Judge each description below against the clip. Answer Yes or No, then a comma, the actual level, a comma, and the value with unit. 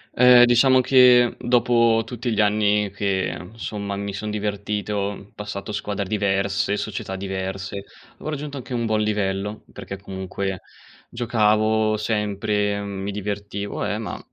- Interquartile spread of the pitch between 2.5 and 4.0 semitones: No, narrow, 2.1 semitones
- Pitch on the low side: Yes, low, 105 Hz